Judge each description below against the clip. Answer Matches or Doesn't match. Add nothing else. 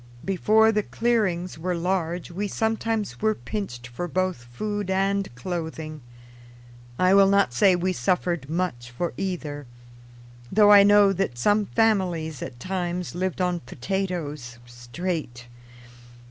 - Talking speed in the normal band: Doesn't match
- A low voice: Doesn't match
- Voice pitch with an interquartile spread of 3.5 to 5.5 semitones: Matches